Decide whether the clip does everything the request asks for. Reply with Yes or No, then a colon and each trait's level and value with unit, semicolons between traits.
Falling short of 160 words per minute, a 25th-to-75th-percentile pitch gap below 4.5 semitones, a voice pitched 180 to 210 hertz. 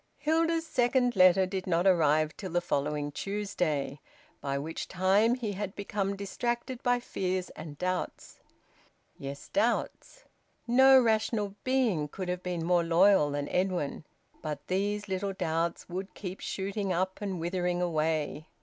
Yes: average, 140 wpm; average, 3.8 semitones; medium, 185 Hz